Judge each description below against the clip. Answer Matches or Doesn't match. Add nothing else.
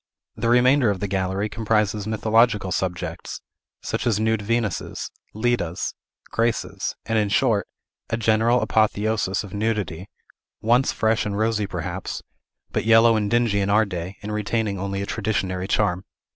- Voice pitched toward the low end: Matches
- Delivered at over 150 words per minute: Doesn't match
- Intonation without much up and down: Matches